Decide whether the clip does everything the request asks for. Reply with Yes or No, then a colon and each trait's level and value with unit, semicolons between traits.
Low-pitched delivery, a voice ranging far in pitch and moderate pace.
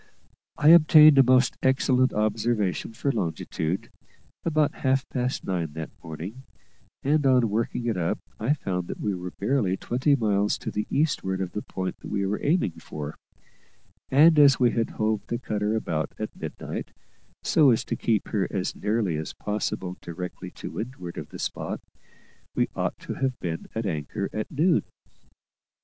Yes: low, 110 Hz; wide, 5.9 semitones; average, 165 wpm